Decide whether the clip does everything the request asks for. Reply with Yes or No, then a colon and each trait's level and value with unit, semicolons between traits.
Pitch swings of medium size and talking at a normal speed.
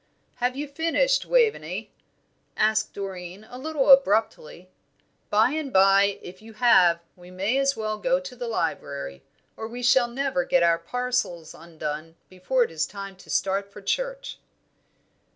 No: wide, 6.3 semitones; average, 150 wpm